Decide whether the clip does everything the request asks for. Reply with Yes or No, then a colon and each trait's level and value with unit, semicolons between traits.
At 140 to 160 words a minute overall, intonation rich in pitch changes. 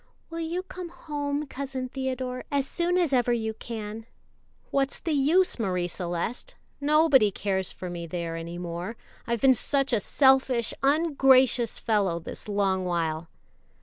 Yes: average, 150 wpm; wide, 7.0 semitones